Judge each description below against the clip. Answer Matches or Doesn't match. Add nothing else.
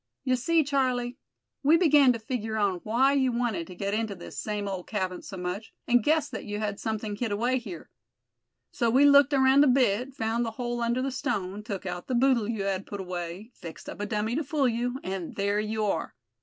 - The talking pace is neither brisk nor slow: Doesn't match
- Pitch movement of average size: Matches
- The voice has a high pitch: Matches